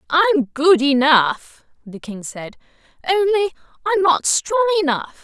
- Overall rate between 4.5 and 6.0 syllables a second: No, 3.9 syllables/s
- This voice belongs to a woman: Yes, female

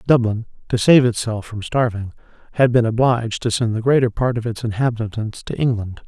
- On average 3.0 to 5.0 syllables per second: No, 5.5 syllables/s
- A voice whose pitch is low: Yes, low, 115 Hz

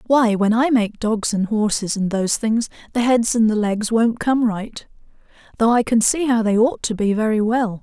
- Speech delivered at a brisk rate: Yes, fast, 220 wpm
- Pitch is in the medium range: No, high, 225 Hz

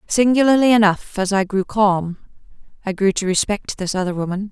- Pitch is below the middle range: No, high, 200 Hz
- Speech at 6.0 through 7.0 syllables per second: No, 5.4 syllables/s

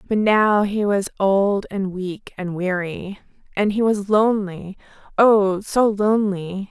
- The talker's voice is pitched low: No, high, 200 Hz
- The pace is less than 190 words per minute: Yes, average, 145 wpm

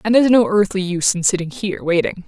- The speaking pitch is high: Yes, high, 195 Hz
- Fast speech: Yes, fast, 240 wpm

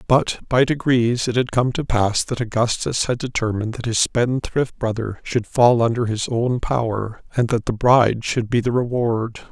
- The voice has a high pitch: No, low, 120 Hz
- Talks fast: No, average, 190 wpm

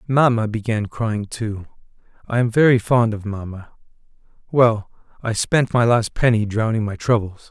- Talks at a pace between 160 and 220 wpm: No, slow, 135 wpm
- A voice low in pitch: Yes, low, 110 Hz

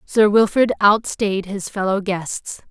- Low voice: No, high, 200 Hz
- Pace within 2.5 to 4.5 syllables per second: Yes, 3.6 syllables/s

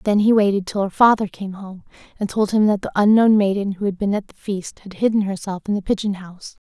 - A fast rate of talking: Yes, fast, 250 wpm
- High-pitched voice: Yes, high, 200 Hz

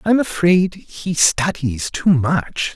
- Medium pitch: Yes, medium, 160 Hz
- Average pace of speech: No, slow, 130 wpm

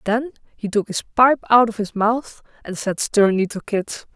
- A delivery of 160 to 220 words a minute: Yes, average, 200 wpm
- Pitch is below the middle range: No, high, 220 Hz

